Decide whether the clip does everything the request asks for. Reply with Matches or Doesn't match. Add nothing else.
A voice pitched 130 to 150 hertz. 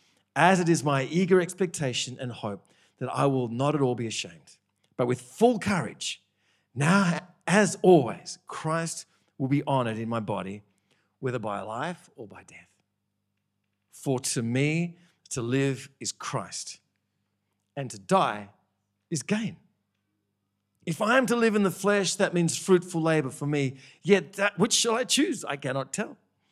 Matches